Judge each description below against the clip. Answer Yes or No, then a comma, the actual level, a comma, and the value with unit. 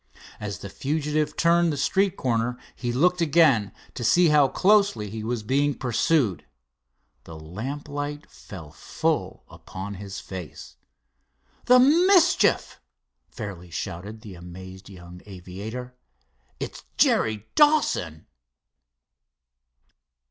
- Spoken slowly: Yes, slow, 110 wpm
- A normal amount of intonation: No, wide, 8.1 semitones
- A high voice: No, low, 120 Hz